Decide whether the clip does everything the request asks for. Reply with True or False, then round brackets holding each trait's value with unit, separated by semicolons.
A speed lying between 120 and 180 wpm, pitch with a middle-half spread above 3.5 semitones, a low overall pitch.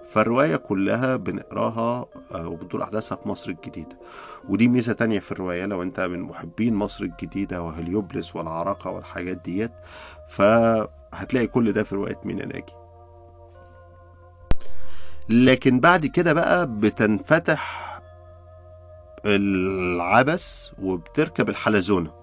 False (105 wpm; 4.3 semitones; 95 Hz)